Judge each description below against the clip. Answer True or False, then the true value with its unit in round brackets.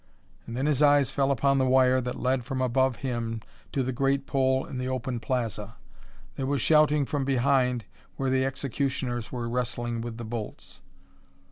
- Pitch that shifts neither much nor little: False (2.2 semitones)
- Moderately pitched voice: False (130 Hz)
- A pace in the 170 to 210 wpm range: True (175 wpm)